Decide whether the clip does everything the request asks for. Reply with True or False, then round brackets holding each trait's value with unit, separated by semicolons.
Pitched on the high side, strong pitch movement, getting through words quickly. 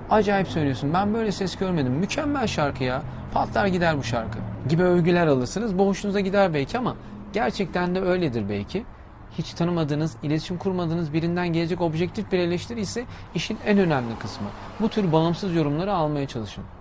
False (170 Hz; 5.7 semitones; 155 wpm)